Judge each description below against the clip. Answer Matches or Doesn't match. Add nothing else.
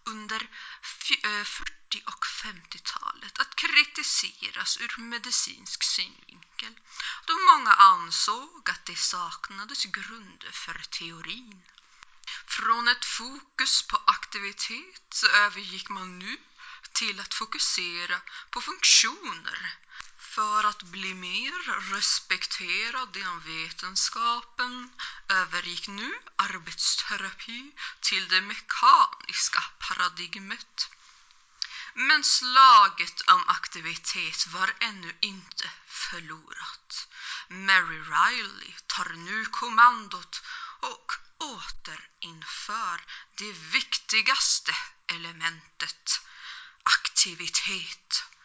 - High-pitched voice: Matches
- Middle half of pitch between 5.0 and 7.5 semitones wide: Matches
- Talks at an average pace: Doesn't match